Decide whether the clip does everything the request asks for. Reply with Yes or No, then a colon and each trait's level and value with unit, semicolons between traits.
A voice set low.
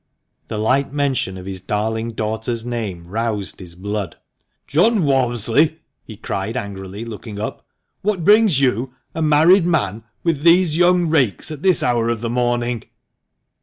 Yes: low, 120 Hz